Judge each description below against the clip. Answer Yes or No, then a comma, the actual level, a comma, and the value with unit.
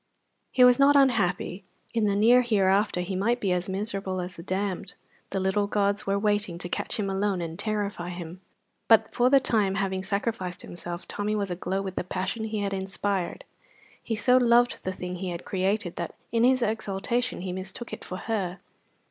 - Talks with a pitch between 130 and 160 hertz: No, high, 200 Hz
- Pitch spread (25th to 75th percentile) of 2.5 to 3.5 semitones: Yes, average, 3.0 semitones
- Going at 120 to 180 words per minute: No, average, 190 wpm